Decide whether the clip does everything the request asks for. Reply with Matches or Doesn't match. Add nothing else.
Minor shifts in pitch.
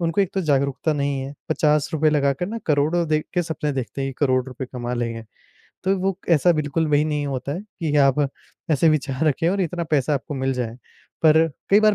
Doesn't match